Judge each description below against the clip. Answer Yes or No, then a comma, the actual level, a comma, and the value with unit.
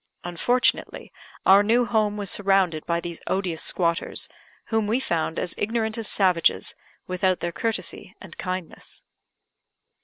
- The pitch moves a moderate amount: Yes, average, 4.1 semitones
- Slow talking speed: Yes, slow, 130 wpm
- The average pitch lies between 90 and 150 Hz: No, high, 190 Hz